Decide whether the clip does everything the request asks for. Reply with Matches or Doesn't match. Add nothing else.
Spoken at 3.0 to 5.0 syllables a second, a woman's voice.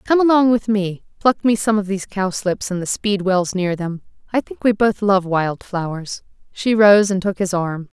Matches